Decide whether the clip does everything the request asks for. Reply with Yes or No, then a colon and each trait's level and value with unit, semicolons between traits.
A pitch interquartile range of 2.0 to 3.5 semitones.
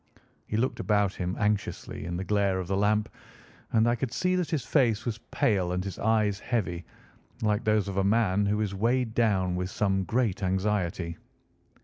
Yes: average, 2.9 semitones